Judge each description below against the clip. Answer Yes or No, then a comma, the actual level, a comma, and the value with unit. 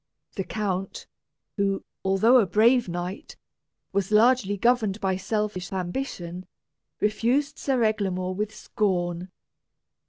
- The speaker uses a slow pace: Yes, slow, 105 wpm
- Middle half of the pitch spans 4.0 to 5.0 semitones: No, average, 3.0 semitones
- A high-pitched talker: Yes, high, 200 Hz